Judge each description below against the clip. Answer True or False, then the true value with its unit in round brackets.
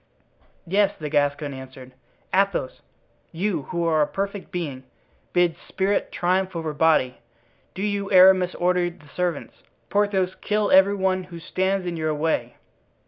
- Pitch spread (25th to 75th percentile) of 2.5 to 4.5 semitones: True (3.5 semitones)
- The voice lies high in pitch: False (180 Hz)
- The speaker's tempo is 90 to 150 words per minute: True (140 wpm)